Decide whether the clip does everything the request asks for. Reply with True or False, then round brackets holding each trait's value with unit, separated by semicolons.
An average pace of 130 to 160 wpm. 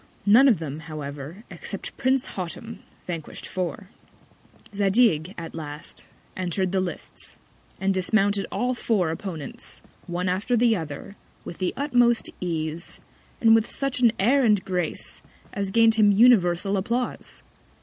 True (140 wpm)